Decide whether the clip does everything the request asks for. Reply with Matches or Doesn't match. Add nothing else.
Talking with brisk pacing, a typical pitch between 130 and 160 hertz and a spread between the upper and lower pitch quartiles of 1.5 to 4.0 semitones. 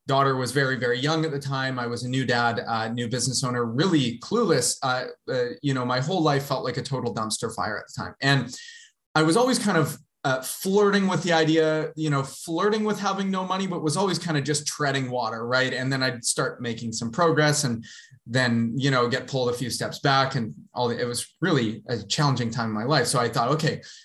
Doesn't match